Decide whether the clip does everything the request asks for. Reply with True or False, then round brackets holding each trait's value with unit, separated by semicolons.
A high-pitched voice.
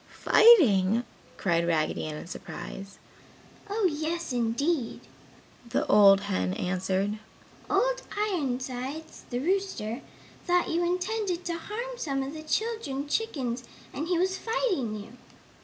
True (285 Hz)